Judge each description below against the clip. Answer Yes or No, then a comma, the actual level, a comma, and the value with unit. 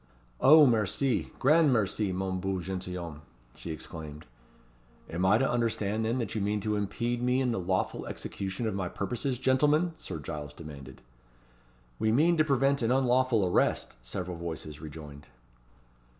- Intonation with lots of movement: Yes, wide, 6.1 semitones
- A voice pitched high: No, low, 105 Hz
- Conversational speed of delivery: Yes, average, 150 wpm